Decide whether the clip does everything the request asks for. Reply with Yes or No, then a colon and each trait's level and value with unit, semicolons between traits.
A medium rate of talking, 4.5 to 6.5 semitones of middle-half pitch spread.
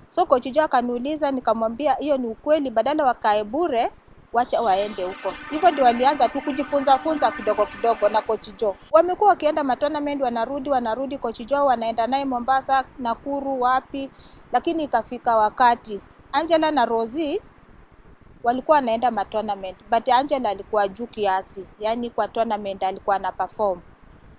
Yes: average, 130 wpm; average, 4.9 semitones